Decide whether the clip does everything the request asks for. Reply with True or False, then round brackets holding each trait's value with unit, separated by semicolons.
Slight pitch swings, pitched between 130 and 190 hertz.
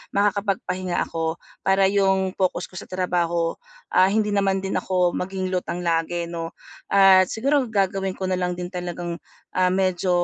True (1.6 semitones; 185 Hz)